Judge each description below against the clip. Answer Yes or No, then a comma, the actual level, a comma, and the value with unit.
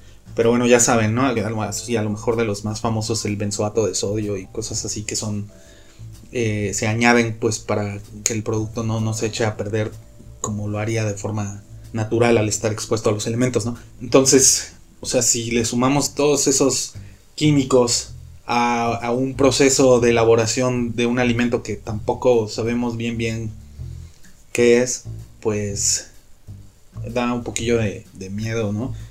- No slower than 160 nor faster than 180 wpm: Yes, average, 165 wpm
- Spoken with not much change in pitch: Yes, narrow, 2.1 semitones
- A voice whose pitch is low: Yes, low, 115 Hz